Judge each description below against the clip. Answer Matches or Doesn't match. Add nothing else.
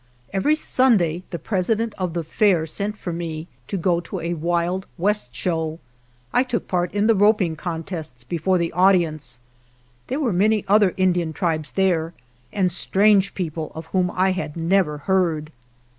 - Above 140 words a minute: Matches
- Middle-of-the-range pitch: Matches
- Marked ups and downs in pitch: Doesn't match